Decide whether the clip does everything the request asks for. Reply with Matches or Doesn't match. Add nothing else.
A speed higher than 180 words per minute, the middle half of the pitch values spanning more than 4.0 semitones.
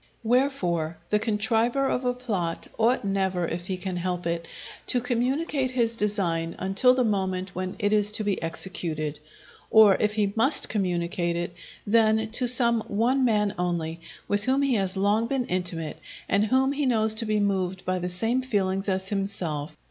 Doesn't match